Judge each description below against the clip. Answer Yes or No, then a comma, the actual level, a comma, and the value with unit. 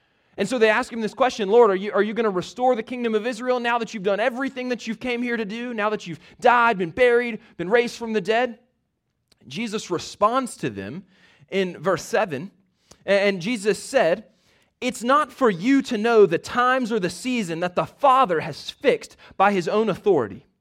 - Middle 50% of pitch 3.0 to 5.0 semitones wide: Yes, average, 3.8 semitones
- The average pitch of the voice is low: No, high, 225 Hz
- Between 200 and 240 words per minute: Yes, fast, 205 wpm